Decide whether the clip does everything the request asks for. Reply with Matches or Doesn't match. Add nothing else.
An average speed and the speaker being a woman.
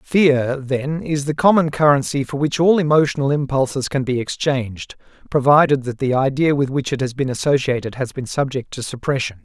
Doesn't match